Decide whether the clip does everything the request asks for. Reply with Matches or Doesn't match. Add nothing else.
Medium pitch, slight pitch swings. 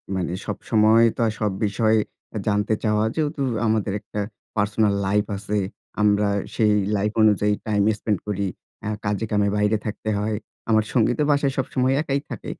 Doesn't match